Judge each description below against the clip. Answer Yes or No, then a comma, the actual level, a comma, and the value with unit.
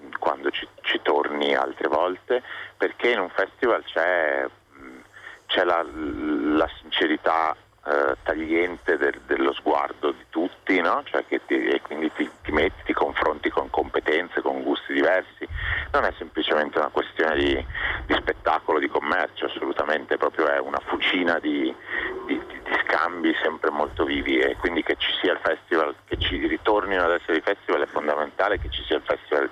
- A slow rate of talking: No, average, 165 wpm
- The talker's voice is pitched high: Yes, very high, 375 Hz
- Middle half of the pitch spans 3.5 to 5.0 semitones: No, wide, 5.6 semitones